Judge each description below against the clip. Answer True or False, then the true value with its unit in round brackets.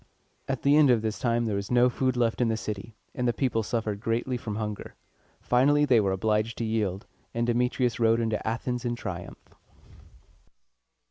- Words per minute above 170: True (185 wpm)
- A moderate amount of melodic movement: False (2.3 semitones)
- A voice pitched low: True (115 Hz)